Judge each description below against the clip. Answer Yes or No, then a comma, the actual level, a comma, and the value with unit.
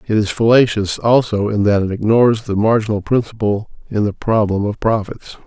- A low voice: Yes, low, 105 Hz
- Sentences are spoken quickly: No, average, 175 wpm